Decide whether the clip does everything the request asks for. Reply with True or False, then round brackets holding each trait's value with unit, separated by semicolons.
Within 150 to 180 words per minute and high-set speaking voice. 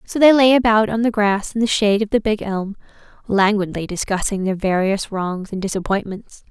False (195 wpm; 205 Hz)